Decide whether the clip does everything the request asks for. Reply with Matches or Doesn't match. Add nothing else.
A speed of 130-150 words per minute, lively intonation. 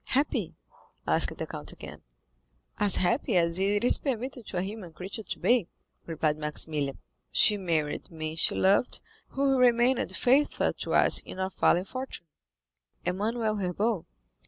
Matches